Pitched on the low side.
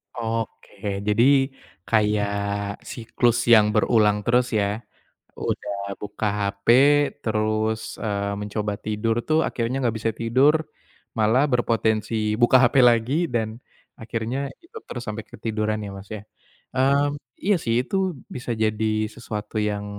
Yes: low, 110 Hz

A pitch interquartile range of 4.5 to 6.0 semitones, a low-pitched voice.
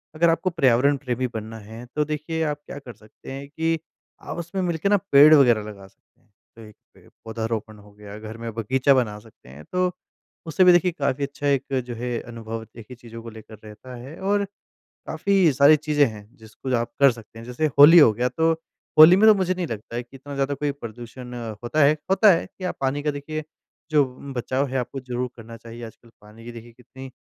Yes: average, 5.0 semitones; low, 130 Hz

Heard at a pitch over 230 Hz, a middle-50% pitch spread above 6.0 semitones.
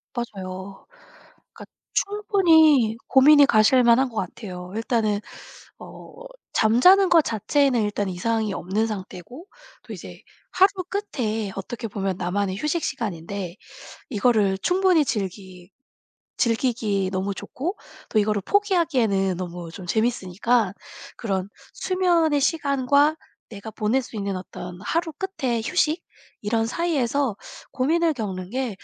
No: high, 225 Hz; wide, 6.7 semitones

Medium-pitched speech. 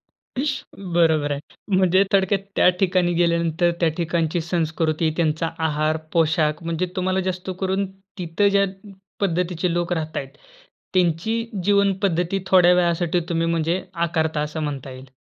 Yes: medium, 170 Hz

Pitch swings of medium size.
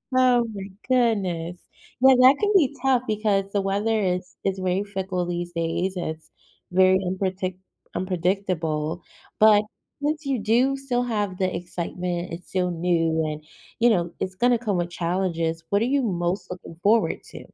Yes: average, 4.3 semitones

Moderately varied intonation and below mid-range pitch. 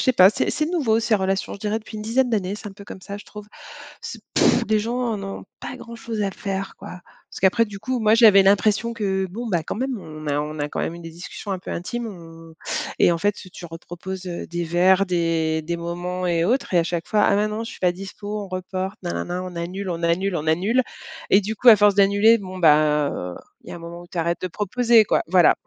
No: average, 3.7 semitones; high, 190 Hz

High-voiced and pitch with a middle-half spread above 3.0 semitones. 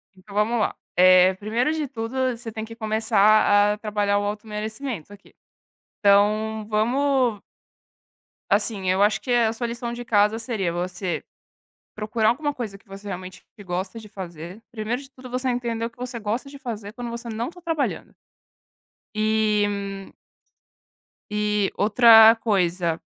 No: high, 215 Hz; average, 2.7 semitones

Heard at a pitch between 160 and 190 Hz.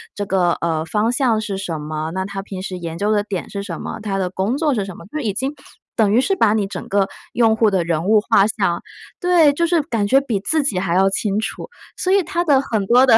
No: high, 205 Hz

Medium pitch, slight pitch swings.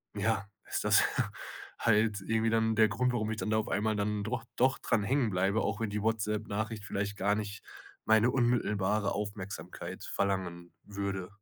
No: low, 105 Hz; narrow, 1.8 semitones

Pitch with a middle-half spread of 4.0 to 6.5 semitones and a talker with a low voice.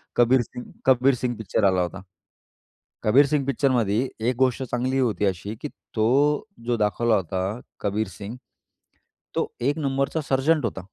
Yes: average, 4.3 semitones; low, 120 Hz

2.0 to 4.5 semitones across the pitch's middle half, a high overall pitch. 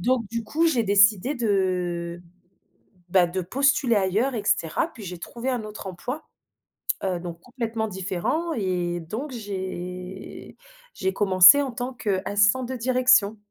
No: average, 5.1 semitones; high, 205 Hz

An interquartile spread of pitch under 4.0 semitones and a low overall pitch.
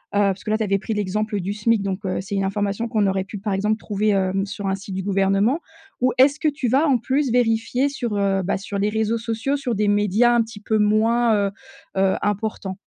No: narrow, 2.6 semitones; high, 210 Hz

